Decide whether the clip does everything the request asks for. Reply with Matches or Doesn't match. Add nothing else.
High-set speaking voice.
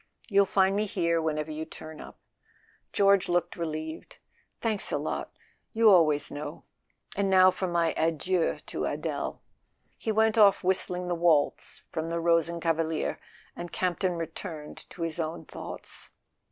Doesn't match